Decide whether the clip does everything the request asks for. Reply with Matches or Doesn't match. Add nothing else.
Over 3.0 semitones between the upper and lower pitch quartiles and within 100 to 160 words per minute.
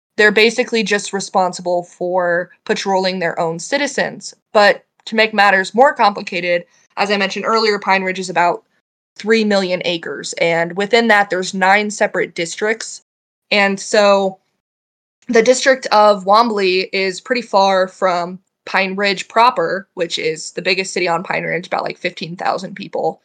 Doesn't match